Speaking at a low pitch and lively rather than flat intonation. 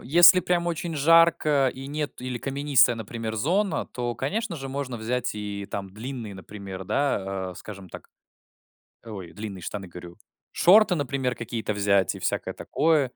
Yes: low, 125 Hz; wide, 6.5 semitones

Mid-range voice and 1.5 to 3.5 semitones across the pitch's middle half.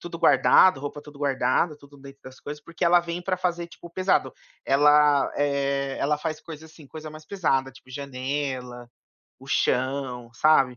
Yes: medium, 145 Hz; average, 2.9 semitones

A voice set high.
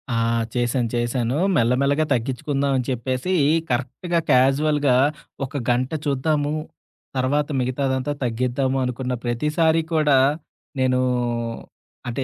No: low, 130 Hz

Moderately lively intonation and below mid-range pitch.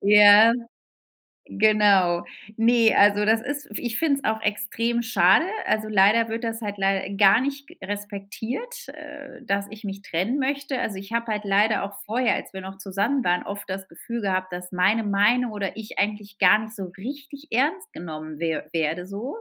No: average, 3.3 semitones; high, 210 Hz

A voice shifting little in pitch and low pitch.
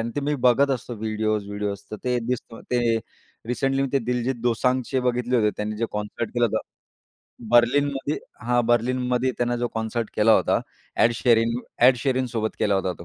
Yes: narrow, 2.3 semitones; low, 120 Hz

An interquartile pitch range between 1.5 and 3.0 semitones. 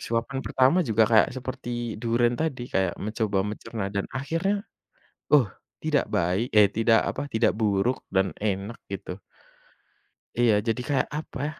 No: average, 3.8 semitones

